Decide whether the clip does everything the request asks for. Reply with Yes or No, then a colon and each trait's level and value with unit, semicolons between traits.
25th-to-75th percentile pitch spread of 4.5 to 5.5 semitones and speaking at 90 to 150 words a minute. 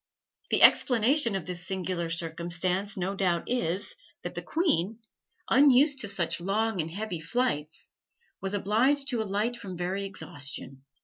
Yes: average, 5.0 semitones; average, 140 wpm